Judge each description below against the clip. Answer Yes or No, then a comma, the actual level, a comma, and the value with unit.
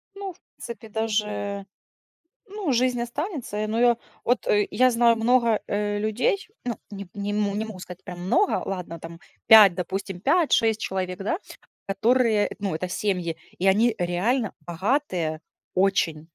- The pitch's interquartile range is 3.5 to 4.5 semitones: Yes, average, 4.0 semitones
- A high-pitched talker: Yes, high, 210 Hz